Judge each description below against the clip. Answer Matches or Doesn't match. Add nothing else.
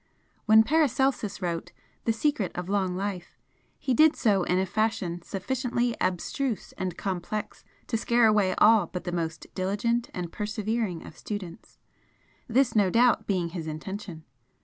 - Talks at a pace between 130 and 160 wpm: Matches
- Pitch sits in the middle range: Doesn't match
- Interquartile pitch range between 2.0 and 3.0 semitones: Doesn't match